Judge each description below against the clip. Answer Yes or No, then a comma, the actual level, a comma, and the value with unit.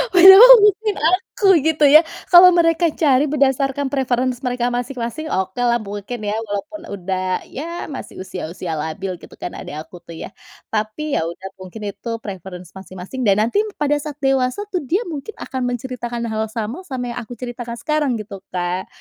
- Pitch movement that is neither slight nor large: No, wide, 7.2 semitones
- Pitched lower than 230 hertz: No, high, 245 Hz